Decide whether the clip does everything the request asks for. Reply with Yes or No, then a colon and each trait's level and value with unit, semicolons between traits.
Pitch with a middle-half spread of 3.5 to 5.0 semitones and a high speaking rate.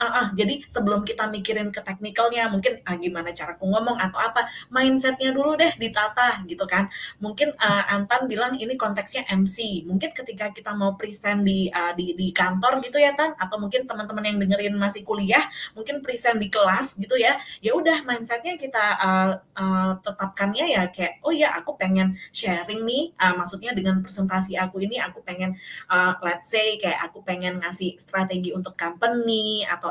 Yes: average, 4.1 semitones; fast, 180 wpm